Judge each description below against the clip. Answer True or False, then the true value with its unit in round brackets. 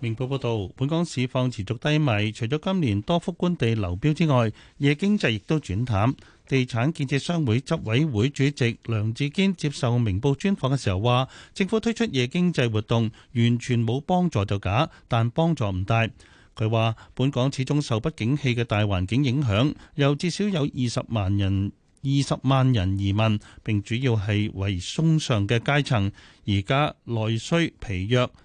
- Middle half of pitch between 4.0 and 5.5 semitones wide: True (5.2 semitones)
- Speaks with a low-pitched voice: True (125 Hz)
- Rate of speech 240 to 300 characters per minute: True (255 characters per minute)